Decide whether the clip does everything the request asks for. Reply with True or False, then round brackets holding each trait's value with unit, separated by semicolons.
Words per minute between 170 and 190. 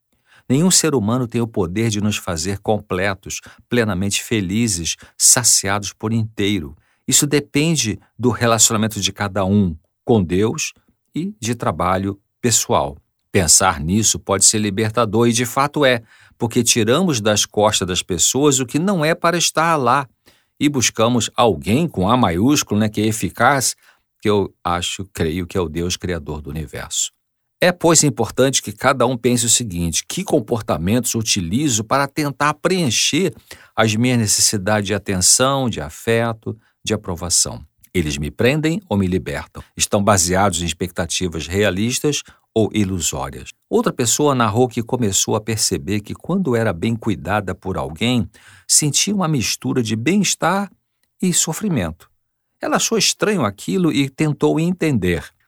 False (150 wpm)